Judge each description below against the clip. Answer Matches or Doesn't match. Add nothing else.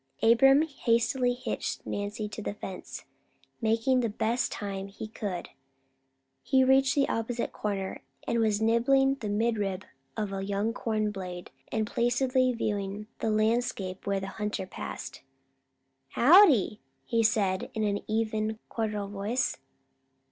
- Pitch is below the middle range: Doesn't match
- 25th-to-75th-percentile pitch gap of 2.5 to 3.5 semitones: Matches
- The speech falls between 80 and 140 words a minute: Matches